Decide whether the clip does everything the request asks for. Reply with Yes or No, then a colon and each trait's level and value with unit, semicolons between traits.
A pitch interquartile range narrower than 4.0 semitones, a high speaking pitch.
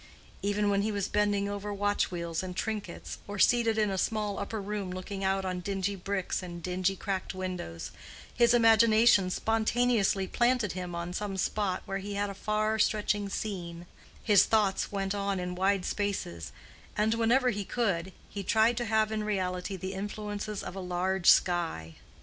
Yes: narrow, 2.4 semitones; high, 200 Hz